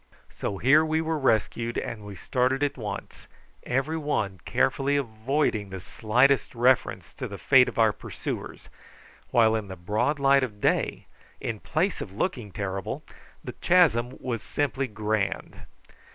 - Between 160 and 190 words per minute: No, average, 150 wpm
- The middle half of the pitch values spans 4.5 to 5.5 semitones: Yes, average, 4.8 semitones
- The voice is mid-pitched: No, low, 120 Hz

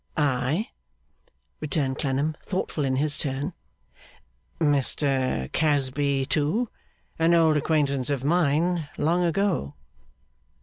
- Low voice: No, medium, 145 Hz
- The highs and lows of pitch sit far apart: No, average, 3.2 semitones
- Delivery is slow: Yes, slow, 95 wpm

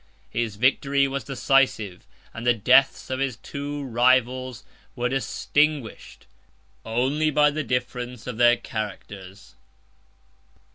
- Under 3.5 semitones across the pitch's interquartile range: Yes, average, 2.7 semitones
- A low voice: Yes, low, 125 Hz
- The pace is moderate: No, slow, 110 wpm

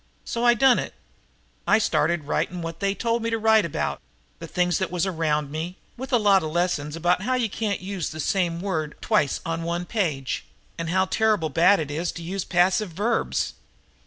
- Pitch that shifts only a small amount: No, average, 3.9 semitones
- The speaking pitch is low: No, medium, 180 Hz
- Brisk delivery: Yes, fast, 210 wpm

